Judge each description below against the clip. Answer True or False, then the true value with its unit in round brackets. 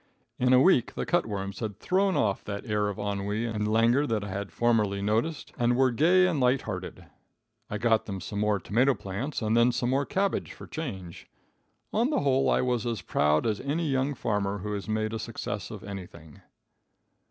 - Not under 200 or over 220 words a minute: True (205 wpm)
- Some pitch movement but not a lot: True (4.5 semitones)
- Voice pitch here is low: True (115 Hz)